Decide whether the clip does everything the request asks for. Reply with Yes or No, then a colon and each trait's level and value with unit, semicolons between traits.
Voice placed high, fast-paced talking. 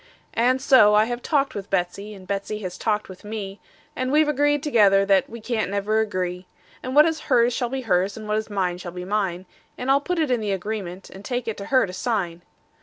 Yes: high, 215 Hz; fast, 240 wpm